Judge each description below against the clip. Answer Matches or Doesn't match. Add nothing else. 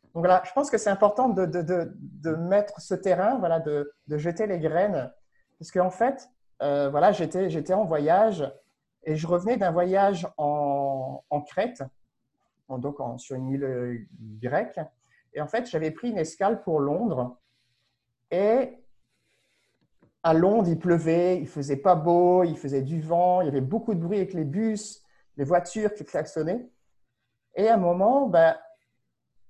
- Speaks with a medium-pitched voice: Matches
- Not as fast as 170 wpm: Doesn't match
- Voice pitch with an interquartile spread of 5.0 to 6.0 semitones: Matches